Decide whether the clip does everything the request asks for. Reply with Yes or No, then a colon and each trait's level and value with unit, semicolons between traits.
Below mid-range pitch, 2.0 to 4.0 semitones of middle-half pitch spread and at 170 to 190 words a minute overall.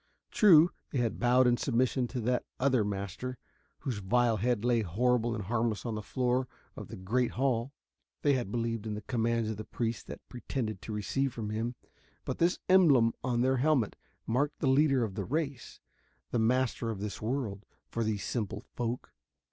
Yes: low, 120 Hz; average, 2.9 semitones; average, 180 wpm